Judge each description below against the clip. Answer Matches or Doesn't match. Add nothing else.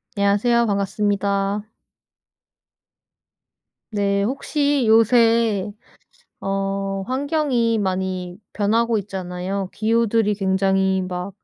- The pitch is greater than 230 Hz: Doesn't match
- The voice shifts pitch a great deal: Doesn't match